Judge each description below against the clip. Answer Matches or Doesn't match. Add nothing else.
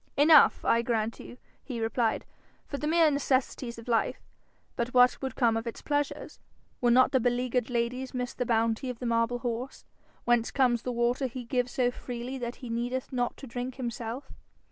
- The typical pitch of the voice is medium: Doesn't match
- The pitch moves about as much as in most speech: Doesn't match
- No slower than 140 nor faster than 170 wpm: Doesn't match